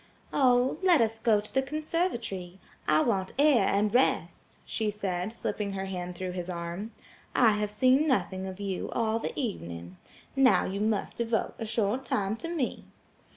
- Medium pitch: No, high, 215 Hz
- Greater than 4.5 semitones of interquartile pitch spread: Yes, average, 4.9 semitones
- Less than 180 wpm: Yes, average, 170 wpm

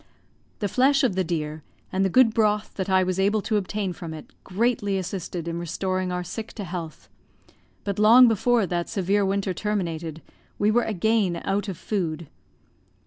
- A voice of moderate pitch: No, high, 195 Hz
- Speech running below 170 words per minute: No, average, 175 wpm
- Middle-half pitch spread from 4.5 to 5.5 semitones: No, average, 3.2 semitones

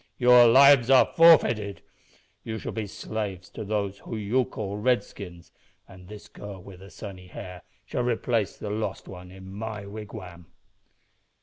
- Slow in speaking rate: No, average, 150 wpm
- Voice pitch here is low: Yes, low, 105 Hz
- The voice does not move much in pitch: No, average, 3.2 semitones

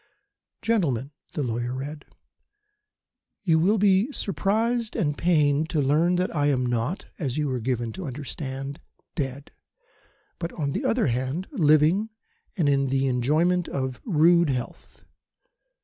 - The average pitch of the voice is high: No, medium, 150 Hz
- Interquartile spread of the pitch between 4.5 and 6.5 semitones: Yes, average, 5.1 semitones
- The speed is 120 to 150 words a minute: Yes, slow, 135 wpm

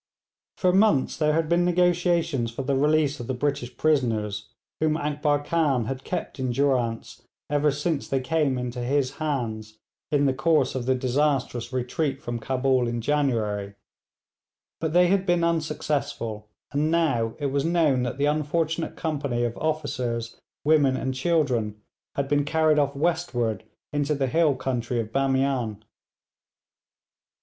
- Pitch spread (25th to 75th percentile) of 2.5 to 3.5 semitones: No, average, 4.0 semitones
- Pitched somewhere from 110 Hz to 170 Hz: Yes, medium, 140 Hz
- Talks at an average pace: Yes, average, 150 wpm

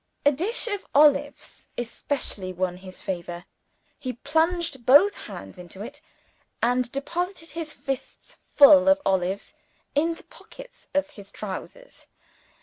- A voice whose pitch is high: Yes, very high, 280 Hz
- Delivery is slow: Yes, slow, 130 wpm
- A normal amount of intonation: No, wide, 8.2 semitones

